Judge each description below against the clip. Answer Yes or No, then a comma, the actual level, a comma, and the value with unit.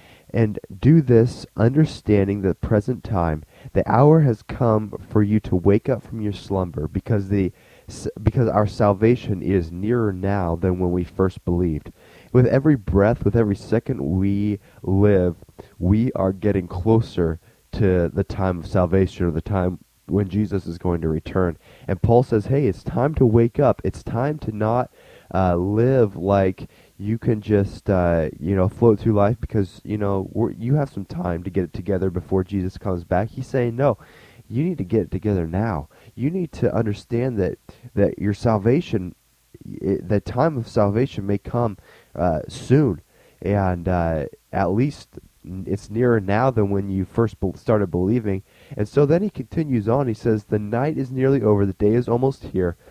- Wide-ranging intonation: No, average, 3.8 semitones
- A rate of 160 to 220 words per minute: Yes, average, 180 wpm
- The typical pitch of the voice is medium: No, low, 105 Hz